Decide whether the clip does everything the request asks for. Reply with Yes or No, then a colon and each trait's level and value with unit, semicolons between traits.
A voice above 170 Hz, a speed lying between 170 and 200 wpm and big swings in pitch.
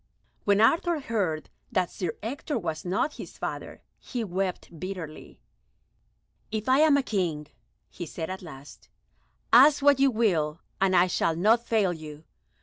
No: high, 190 Hz; average, 145 wpm; wide, 6.1 semitones